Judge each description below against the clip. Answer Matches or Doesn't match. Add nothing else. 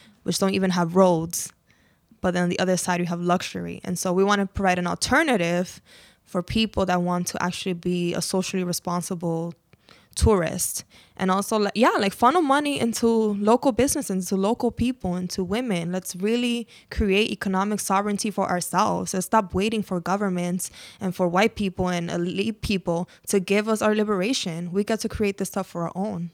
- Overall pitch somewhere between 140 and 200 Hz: Matches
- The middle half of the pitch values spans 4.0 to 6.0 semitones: Doesn't match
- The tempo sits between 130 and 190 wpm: Matches